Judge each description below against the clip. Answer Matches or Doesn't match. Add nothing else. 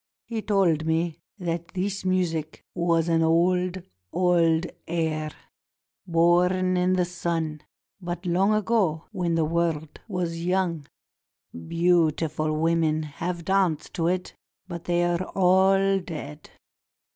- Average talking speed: Doesn't match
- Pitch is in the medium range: Matches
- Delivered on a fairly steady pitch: Matches